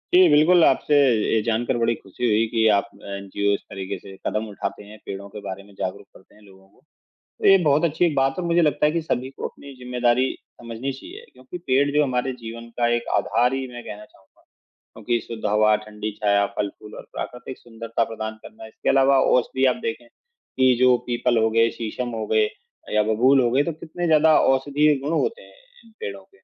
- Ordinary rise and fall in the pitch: Yes, average, 4.5 semitones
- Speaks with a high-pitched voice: No, low, 120 Hz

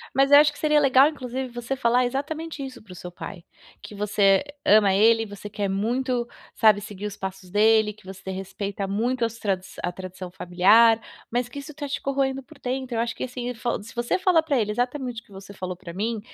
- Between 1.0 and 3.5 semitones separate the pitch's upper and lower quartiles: No, average, 4.8 semitones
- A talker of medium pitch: No, high, 230 Hz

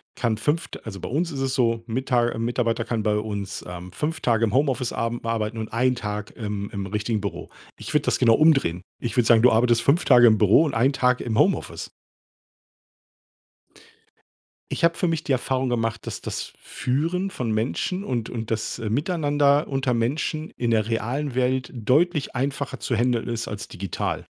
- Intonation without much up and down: No, average, 3.6 semitones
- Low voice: Yes, low, 120 Hz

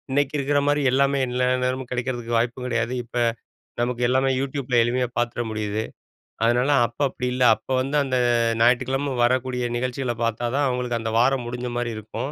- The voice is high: No, low, 125 Hz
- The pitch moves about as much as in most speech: No, narrow, 1.8 semitones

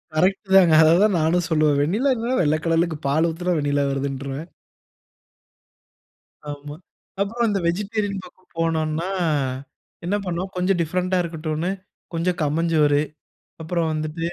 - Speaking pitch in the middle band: Yes, medium, 165 Hz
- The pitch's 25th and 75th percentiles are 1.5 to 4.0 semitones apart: Yes, average, 2.9 semitones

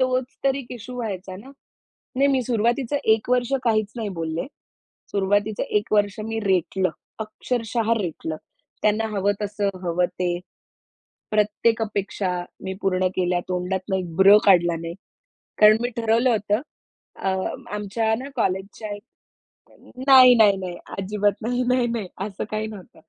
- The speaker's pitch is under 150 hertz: No, high, 210 Hz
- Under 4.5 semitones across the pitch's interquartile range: Yes, average, 3.3 semitones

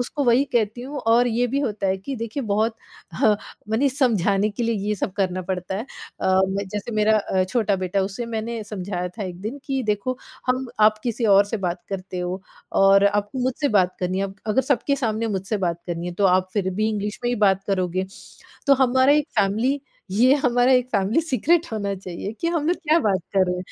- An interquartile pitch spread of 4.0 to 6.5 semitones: Yes, average, 4.3 semitones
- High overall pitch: Yes, high, 210 Hz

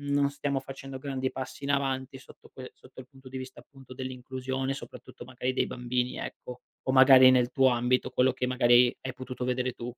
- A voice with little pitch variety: Yes, narrow, 0.9 semitones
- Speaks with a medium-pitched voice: No, low, 130 Hz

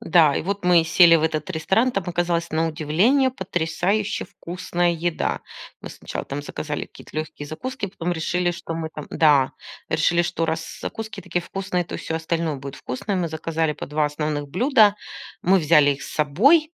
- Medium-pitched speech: Yes, medium, 165 Hz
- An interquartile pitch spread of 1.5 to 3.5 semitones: Yes, average, 3.1 semitones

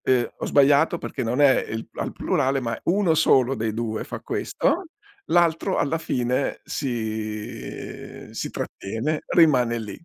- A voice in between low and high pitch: No, low, 130 Hz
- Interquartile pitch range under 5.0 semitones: No, wide, 5.6 semitones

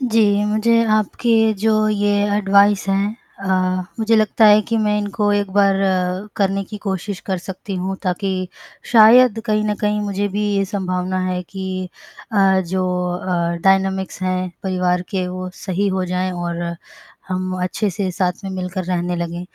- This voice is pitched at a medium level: No, high, 195 Hz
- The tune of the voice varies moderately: No, narrow, 2.1 semitones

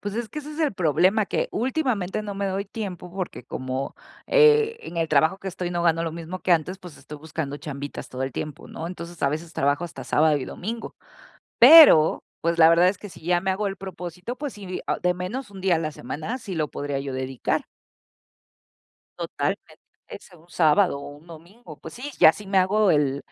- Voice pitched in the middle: Yes, medium, 175 Hz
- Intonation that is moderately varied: Yes, average, 4.4 semitones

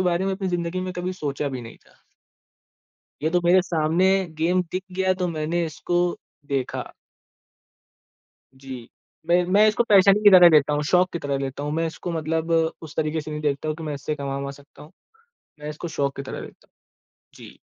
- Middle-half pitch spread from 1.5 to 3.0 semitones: No, average, 3.4 semitones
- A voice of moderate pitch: Yes, medium, 160 Hz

